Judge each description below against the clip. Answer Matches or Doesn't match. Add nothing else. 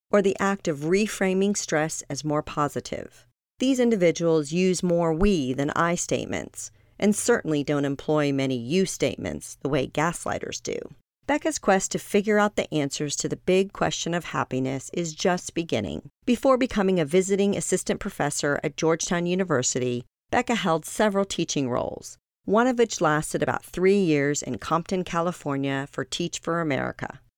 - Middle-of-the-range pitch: Matches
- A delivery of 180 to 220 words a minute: Doesn't match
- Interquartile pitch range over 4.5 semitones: Matches